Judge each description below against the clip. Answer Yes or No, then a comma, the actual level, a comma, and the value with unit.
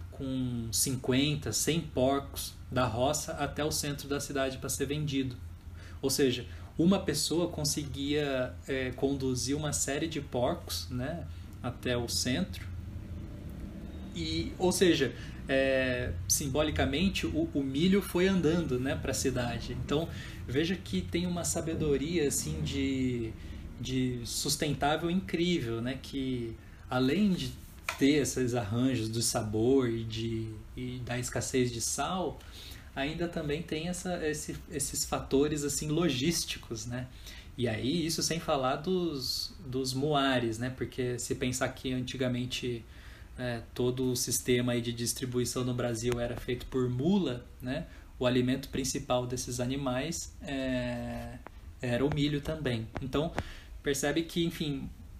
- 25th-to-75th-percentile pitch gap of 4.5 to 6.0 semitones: No, average, 3.7 semitones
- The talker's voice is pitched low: Yes, low, 125 Hz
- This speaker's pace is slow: No, average, 130 wpm